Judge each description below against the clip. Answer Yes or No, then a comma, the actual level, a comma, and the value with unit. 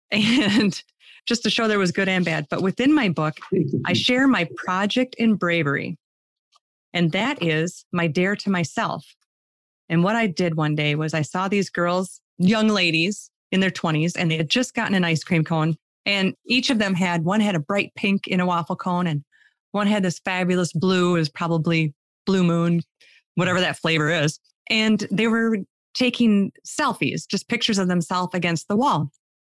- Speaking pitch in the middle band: Yes, medium, 180 Hz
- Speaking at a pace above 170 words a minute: Yes, average, 185 wpm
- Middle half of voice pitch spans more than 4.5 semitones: No, average, 3.8 semitones